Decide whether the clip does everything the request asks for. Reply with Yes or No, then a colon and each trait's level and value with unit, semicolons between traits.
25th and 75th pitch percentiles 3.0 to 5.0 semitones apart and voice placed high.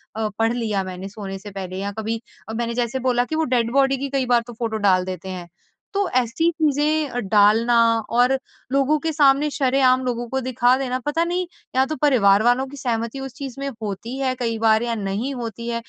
Yes: average, 3.5 semitones; high, 240 Hz